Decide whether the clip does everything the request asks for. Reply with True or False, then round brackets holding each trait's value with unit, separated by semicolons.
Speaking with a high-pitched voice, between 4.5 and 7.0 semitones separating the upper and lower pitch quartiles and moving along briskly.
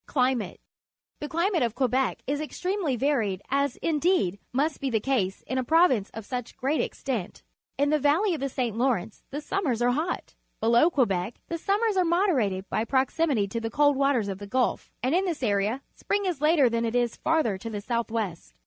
True (260 Hz; 5.3 semitones; 210 wpm)